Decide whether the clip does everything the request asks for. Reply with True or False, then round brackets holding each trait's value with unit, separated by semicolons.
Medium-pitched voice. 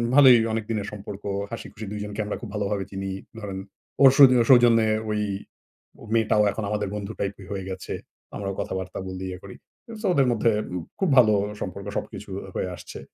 False (105 Hz)